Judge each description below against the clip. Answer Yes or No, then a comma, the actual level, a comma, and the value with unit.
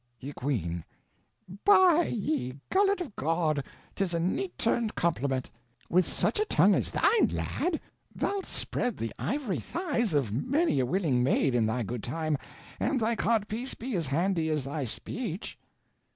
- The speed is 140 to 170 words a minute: Yes, average, 160 wpm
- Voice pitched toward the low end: No, medium, 175 Hz